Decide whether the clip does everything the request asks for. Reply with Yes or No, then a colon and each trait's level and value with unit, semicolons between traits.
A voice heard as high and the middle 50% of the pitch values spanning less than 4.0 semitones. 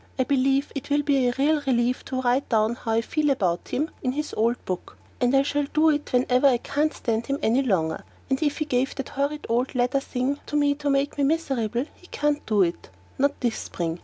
Yes: very high, 270 Hz; average, 3.1 semitones